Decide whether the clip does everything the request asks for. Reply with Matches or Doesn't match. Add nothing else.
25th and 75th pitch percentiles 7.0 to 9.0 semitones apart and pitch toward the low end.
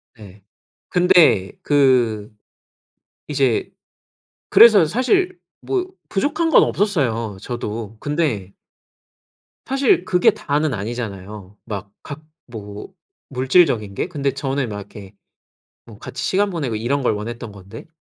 Matches